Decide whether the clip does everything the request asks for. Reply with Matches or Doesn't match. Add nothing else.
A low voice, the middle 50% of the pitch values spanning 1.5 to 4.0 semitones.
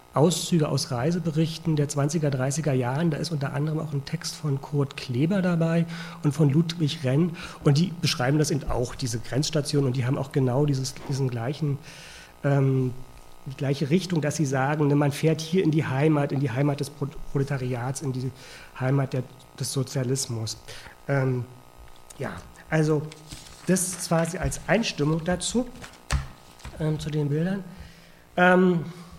Doesn't match